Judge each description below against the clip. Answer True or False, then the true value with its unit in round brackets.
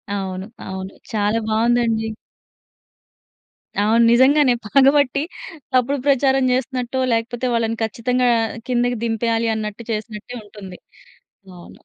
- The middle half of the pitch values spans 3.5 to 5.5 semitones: False (2.8 semitones)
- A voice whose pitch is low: False (230 Hz)